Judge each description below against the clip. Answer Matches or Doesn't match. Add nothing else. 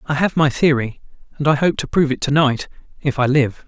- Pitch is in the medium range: Matches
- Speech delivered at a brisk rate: Matches